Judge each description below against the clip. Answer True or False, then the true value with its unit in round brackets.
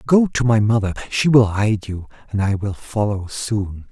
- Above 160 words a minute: True (200 wpm)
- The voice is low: True (110 Hz)